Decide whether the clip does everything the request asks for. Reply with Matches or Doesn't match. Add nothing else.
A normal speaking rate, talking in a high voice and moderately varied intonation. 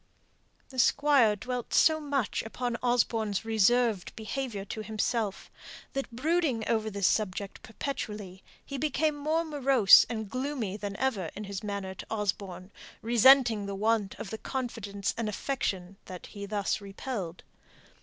Matches